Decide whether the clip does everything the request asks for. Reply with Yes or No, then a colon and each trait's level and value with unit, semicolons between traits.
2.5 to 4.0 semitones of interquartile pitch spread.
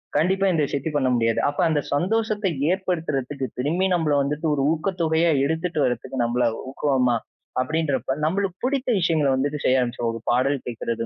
No: average, 4.7 semitones